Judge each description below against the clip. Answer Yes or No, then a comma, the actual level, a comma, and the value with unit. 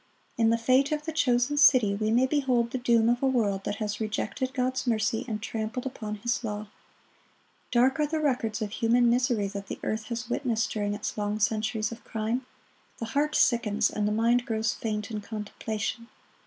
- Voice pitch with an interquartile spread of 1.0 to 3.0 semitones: Yes, average, 2.7 semitones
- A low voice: No, high, 230 Hz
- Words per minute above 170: Yes, average, 190 wpm